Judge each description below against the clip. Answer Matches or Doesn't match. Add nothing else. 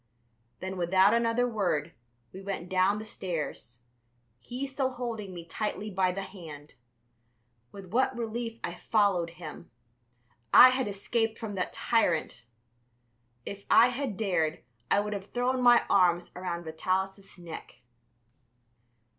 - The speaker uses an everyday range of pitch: Matches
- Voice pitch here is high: Matches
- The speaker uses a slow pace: Matches